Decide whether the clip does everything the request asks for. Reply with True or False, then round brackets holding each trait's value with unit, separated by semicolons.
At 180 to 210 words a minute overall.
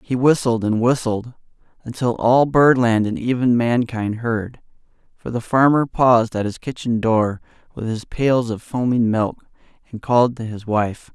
False (160 wpm)